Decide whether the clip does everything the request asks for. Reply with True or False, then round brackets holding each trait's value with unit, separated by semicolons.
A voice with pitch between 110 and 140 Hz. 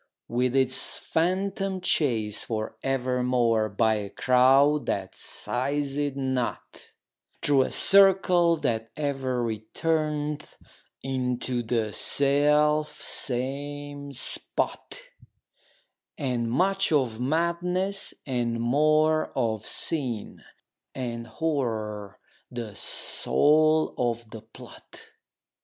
True (135 Hz)